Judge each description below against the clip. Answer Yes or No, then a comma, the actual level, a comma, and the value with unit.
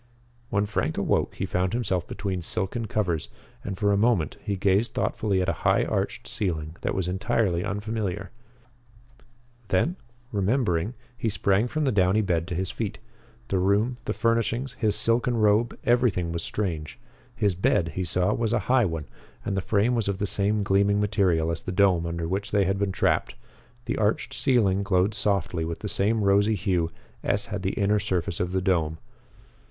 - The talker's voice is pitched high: No, low, 100 Hz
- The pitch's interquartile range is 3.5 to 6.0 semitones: No, average, 2.9 semitones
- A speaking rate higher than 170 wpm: Yes, average, 180 wpm